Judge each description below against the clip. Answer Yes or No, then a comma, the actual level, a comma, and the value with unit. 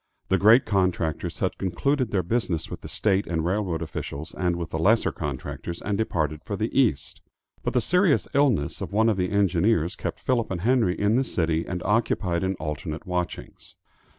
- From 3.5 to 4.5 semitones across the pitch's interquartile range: No, average, 4.9 semitones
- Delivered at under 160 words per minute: No, average, 185 wpm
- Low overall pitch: Yes, very low, 95 Hz